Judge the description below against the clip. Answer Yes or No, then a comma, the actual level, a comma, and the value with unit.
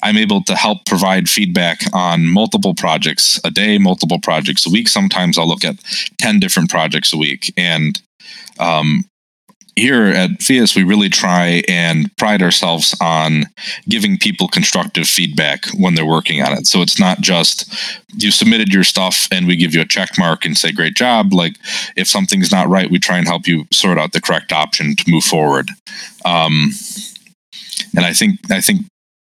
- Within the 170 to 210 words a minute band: Yes, average, 180 wpm